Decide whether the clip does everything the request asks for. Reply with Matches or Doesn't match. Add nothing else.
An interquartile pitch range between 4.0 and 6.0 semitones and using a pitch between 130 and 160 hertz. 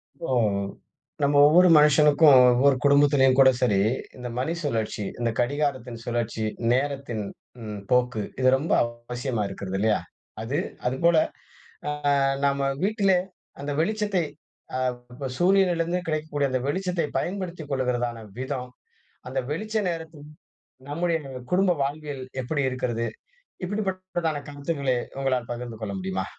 Matches